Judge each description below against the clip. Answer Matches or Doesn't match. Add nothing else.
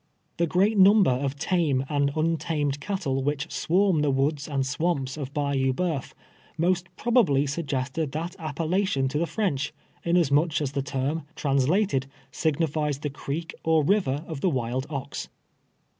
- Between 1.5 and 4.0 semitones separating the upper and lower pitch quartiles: Matches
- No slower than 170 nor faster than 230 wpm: Doesn't match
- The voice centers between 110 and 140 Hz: Doesn't match